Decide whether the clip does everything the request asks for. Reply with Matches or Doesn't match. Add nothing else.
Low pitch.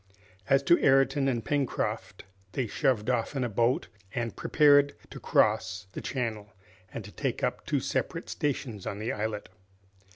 Matches